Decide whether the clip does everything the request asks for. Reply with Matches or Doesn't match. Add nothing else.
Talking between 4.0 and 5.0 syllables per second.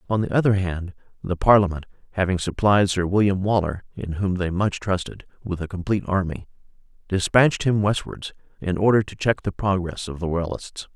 Doesn't match